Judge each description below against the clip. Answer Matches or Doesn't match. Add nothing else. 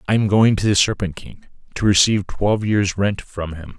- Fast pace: Matches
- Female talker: Doesn't match